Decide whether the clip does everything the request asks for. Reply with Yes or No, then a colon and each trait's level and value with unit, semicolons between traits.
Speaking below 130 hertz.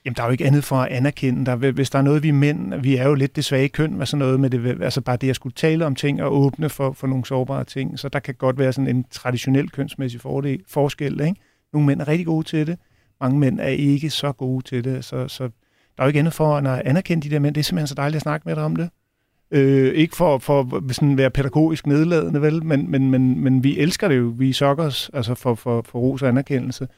No: low, 135 Hz